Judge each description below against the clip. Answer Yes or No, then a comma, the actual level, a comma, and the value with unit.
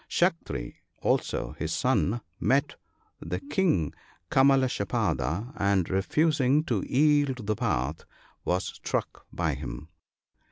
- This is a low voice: Yes, low, 125 Hz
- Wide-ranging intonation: Yes, wide, 8.2 semitones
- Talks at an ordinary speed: No, slow, 105 wpm